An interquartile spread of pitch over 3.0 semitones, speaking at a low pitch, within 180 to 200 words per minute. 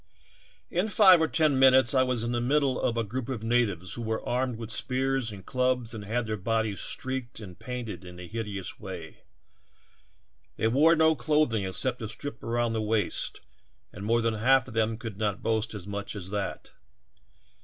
Yes: average, 3.5 semitones; low, 115 Hz; average, 190 wpm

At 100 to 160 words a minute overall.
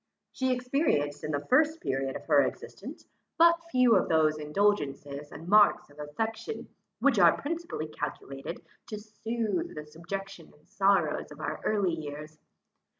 Yes: average, 150 wpm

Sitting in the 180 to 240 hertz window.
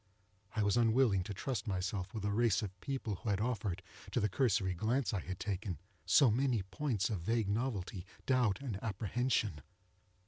No: low, 105 Hz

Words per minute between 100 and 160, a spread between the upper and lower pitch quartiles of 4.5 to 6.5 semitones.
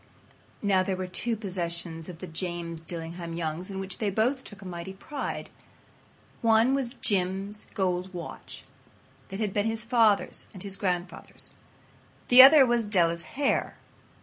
No: average, 150 wpm; average, 4.1 semitones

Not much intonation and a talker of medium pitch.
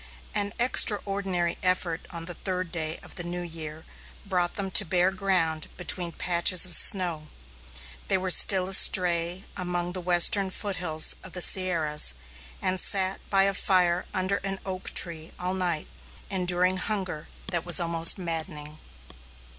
Yes: narrow, 1.9 semitones; medium, 180 Hz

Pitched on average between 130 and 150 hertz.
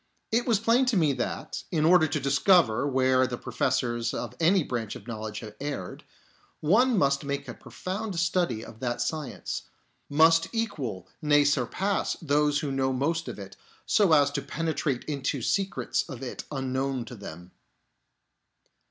Yes: medium, 140 Hz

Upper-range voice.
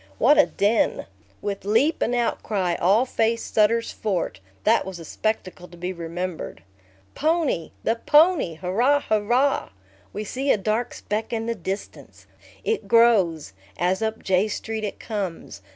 Yes: high, 215 Hz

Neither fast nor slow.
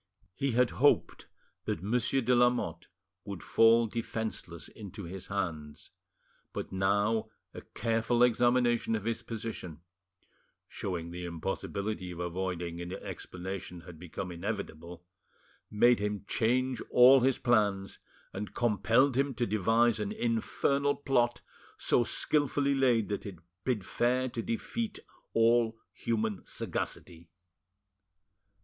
No: slow, 120 wpm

